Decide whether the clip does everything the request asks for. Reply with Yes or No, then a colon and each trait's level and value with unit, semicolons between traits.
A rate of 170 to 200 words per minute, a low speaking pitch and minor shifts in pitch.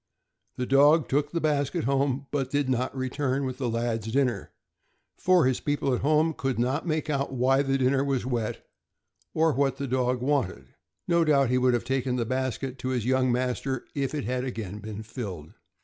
Yes: average, 195 wpm; low, 130 Hz; narrow, 2.2 semitones